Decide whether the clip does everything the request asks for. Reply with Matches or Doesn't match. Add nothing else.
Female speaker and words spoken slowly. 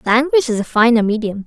Doesn't match